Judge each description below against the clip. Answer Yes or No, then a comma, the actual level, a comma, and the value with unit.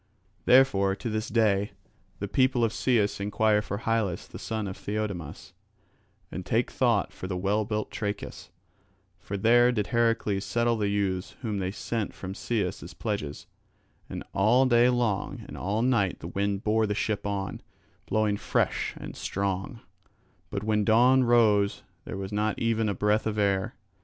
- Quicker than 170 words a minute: No, average, 165 wpm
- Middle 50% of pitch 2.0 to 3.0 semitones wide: Yes, narrow, 2.5 semitones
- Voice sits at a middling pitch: No, low, 105 Hz